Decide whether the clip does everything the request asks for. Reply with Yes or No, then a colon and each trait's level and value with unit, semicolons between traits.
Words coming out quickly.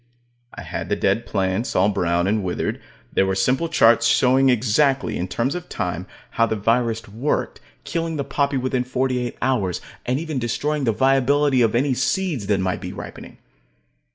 No: average, 180 wpm